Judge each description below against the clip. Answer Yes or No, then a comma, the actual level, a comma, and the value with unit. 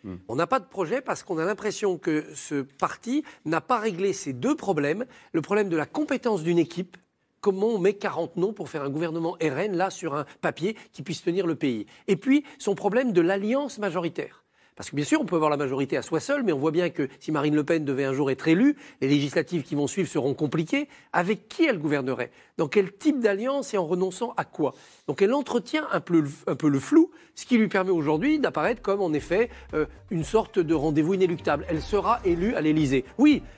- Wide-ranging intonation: Yes, wide, 5.9 semitones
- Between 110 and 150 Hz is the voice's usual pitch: No, medium, 180 Hz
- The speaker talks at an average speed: No, fast, 225 wpm